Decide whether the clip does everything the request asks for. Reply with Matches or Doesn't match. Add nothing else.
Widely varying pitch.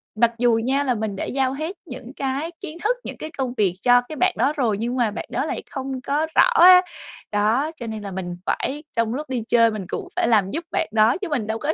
Doesn't match